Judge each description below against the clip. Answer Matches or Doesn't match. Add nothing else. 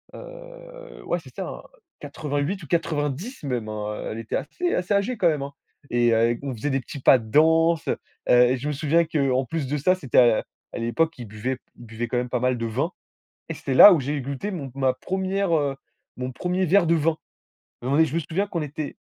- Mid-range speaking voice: Matches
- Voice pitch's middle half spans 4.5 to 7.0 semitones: Matches